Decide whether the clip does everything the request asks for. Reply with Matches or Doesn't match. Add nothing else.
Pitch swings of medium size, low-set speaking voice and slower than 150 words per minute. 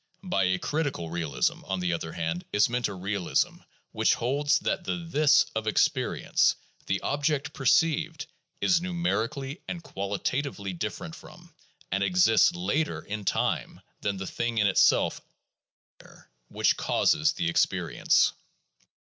Doesn't match